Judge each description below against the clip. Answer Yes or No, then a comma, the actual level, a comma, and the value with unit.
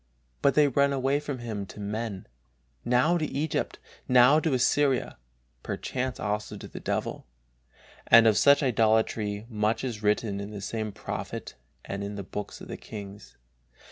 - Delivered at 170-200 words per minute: No, average, 160 wpm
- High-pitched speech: No, low, 115 Hz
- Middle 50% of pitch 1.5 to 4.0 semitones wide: No, average, 4.6 semitones